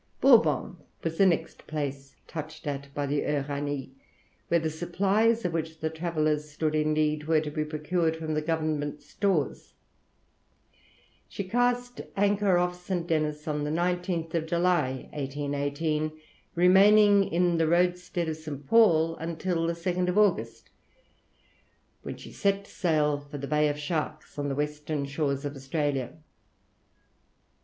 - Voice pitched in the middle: Yes, medium, 160 Hz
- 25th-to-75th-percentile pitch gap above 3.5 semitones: No, average, 3.1 semitones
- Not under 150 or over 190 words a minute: No, average, 140 wpm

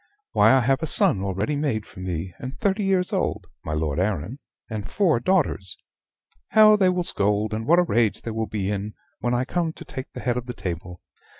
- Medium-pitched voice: No, low, 115 Hz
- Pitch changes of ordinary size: No, wide, 8.4 semitones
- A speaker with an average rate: No, fast, 215 wpm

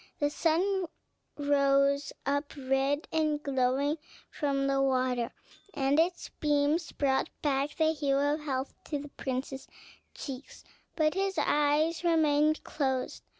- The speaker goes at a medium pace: No, slow, 125 wpm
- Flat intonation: Yes, narrow, 2.1 semitones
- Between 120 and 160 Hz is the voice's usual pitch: No, very high, 285 Hz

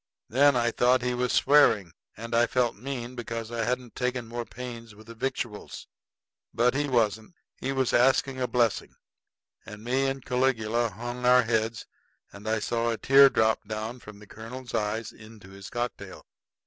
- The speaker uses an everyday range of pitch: No, narrow, 2.2 semitones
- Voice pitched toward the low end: Yes, low, 120 Hz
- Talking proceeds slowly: No, average, 170 wpm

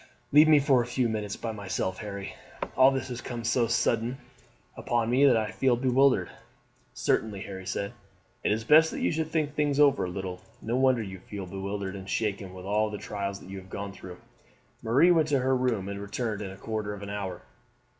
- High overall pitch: No, low, 110 Hz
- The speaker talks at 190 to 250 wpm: Yes, fast, 205 wpm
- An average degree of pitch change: Yes, average, 4.7 semitones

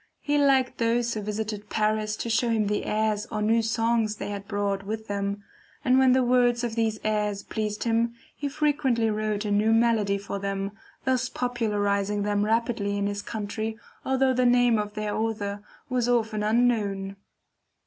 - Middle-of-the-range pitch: No, high, 220 Hz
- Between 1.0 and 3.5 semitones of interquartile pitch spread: Yes, narrow, 2.5 semitones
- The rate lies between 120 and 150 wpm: No, average, 175 wpm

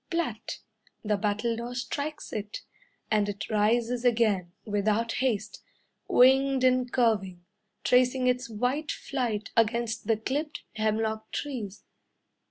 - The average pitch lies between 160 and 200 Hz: No, high, 230 Hz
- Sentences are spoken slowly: Yes, slow, 110 wpm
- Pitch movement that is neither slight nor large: Yes, average, 3.1 semitones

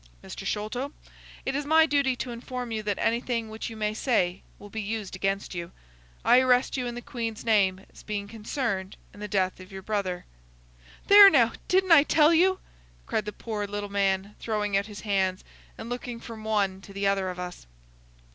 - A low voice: No, high, 215 Hz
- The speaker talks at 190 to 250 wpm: Yes, average, 195 wpm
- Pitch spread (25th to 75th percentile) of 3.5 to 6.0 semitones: Yes, average, 3.8 semitones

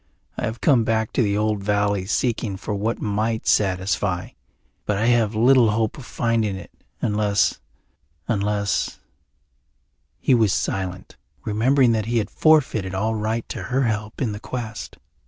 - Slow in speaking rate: No, average, 155 wpm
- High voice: No, low, 110 Hz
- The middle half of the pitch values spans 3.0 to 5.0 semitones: No, narrow, 2.4 semitones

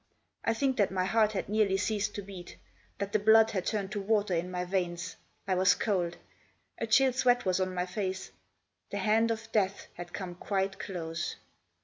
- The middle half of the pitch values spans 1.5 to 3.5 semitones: Yes, average, 3.0 semitones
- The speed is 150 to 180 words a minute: No, average, 195 wpm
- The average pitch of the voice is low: No, high, 195 Hz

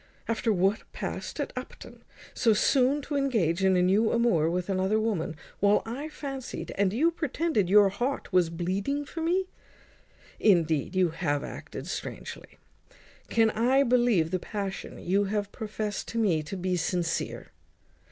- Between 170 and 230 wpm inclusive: No, average, 150 wpm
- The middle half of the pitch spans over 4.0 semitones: Yes, average, 5.1 semitones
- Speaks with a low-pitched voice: No, high, 205 Hz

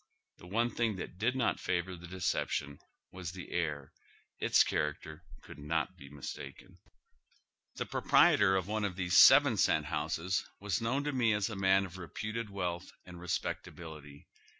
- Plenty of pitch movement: No, average, 4.2 semitones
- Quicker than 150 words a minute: Yes, average, 165 wpm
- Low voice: Yes, very low, 95 Hz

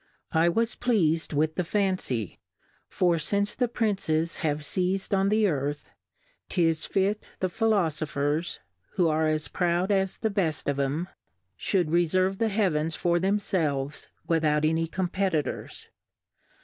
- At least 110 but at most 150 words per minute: Yes, slow, 135 wpm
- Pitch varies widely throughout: No, average, 3.8 semitones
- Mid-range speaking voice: Yes, medium, 170 Hz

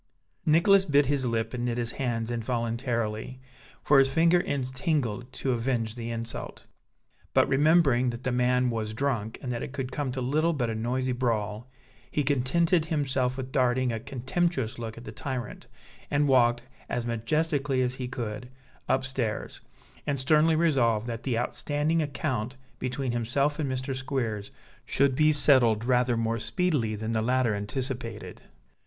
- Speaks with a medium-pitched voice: No, low, 125 Hz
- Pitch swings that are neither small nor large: Yes, average, 3.2 semitones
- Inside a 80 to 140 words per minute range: No, average, 160 wpm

